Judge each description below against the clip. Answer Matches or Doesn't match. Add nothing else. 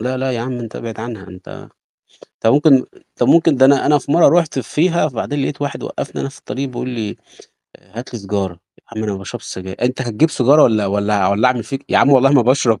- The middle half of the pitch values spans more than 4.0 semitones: Matches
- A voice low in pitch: Matches